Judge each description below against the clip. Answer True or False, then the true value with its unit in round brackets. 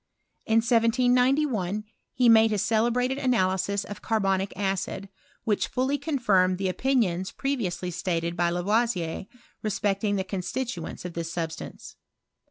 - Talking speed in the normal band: False (115 wpm)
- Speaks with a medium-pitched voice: False (205 Hz)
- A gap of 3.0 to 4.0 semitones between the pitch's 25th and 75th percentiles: False (4.6 semitones)